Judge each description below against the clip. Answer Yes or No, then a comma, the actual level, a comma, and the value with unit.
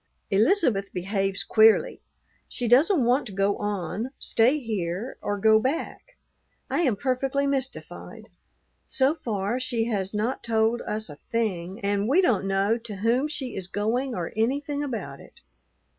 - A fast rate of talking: No, average, 150 wpm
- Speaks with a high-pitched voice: Yes, high, 225 Hz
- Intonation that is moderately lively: Yes, average, 4.6 semitones